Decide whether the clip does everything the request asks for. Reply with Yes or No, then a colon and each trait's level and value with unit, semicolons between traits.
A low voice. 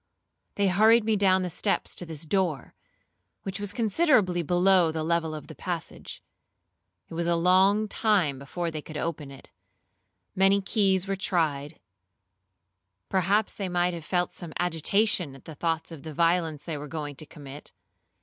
No: medium, 175 Hz